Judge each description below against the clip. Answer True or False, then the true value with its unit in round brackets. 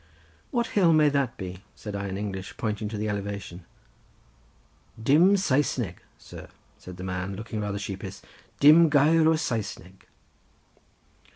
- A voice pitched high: False (105 Hz)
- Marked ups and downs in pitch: True (7.2 semitones)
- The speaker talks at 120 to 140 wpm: True (135 wpm)